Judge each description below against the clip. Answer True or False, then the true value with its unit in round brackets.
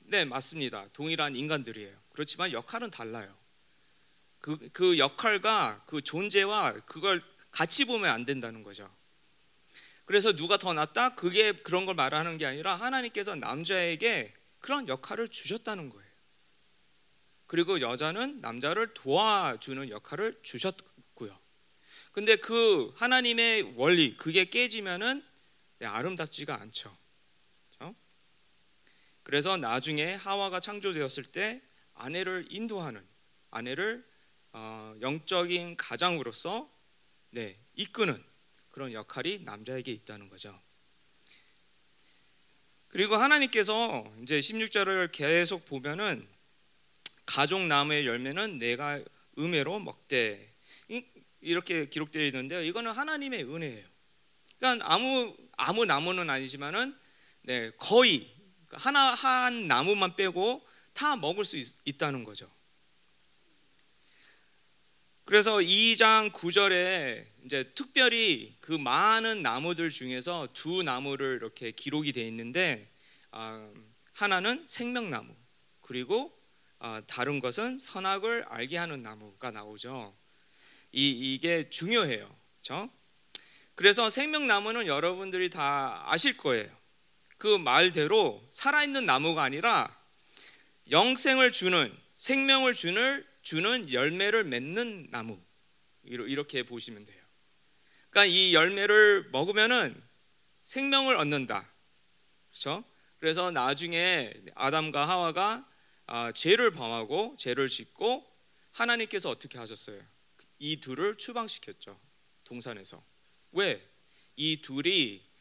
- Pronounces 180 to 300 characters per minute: True (245 characters per minute)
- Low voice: False (170 Hz)